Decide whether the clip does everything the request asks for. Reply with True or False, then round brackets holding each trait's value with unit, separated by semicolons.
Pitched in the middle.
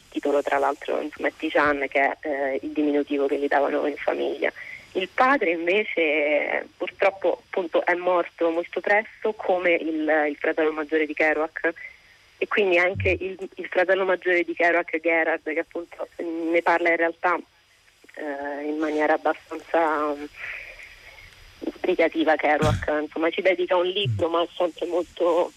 True (160 Hz)